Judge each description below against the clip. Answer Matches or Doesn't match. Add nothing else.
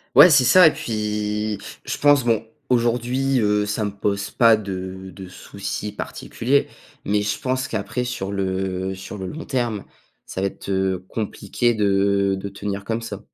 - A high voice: Doesn't match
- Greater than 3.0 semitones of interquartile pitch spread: Matches